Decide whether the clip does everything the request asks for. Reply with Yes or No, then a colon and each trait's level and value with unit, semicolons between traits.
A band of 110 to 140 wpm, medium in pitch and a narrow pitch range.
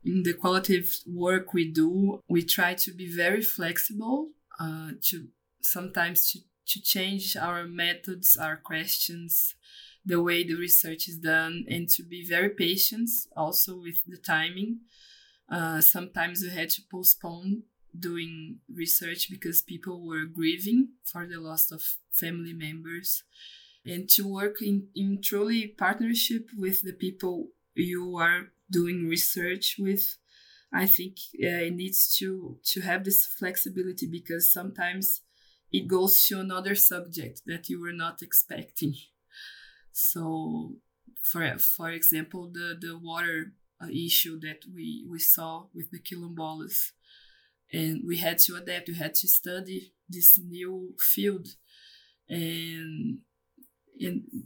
Yes: slow, 135 wpm; medium, 175 Hz; narrow, 2.3 semitones